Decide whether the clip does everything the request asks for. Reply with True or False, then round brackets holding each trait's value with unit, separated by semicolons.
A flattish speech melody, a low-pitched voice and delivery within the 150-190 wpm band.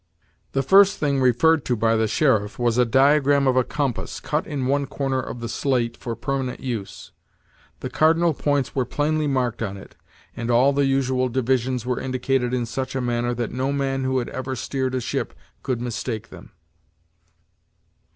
True (2.2 semitones; 130 Hz; 180 wpm)